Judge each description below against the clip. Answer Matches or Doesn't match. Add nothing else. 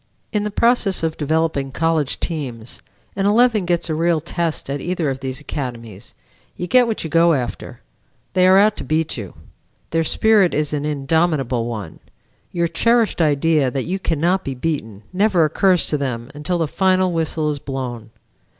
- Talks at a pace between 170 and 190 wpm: Matches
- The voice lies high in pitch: Doesn't match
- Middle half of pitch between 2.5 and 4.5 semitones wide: Doesn't match